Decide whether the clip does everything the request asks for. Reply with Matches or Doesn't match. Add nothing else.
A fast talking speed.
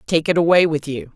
Matches